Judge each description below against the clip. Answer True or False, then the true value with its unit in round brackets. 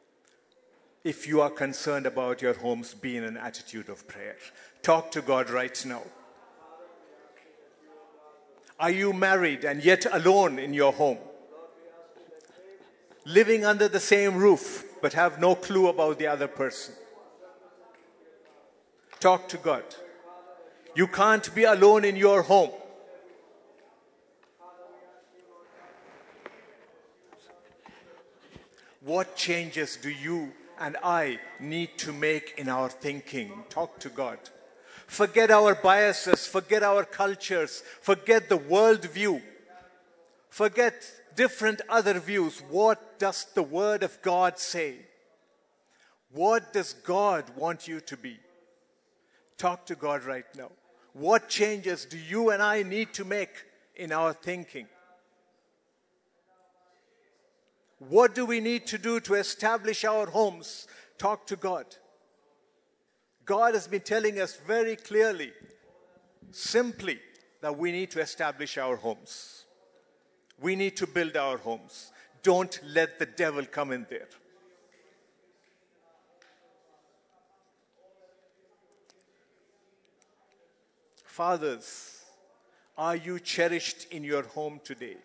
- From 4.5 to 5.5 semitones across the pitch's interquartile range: True (5.0 semitones)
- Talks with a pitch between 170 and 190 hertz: True (185 Hz)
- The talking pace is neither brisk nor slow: False (110 wpm)